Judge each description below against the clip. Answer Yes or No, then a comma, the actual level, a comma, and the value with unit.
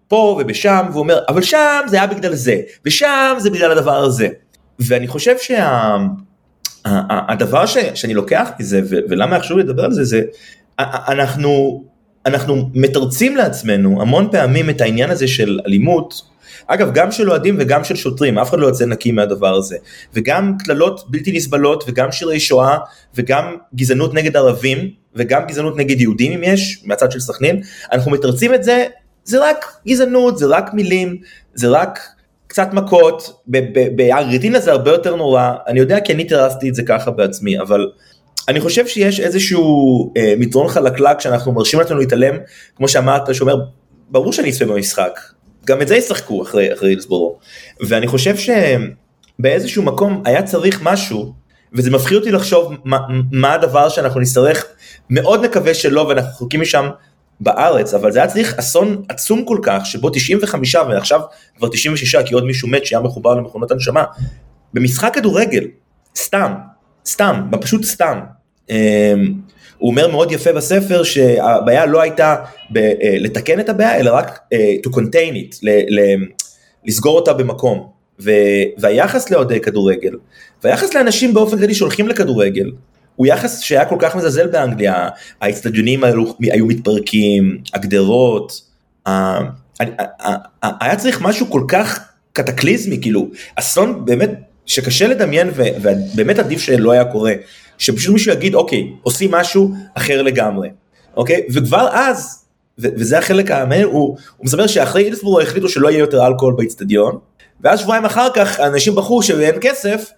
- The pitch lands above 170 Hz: No, medium, 145 Hz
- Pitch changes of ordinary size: No, wide, 7.7 semitones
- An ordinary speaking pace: No, fast, 155 wpm